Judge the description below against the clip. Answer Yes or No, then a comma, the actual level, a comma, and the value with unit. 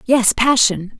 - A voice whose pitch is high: Yes, high, 235 Hz